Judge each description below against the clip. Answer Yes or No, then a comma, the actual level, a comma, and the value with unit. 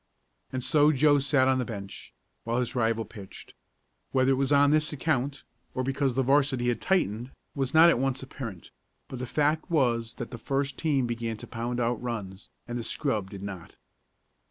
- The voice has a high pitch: No, low, 130 Hz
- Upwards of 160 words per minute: Yes, average, 190 wpm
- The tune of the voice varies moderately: Yes, average, 3.3 semitones